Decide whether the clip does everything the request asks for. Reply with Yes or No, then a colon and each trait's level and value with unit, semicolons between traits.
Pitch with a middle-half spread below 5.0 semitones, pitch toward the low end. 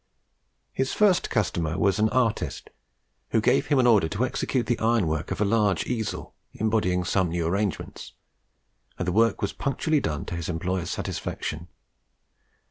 No: average, 5.3 semitones; low, 105 Hz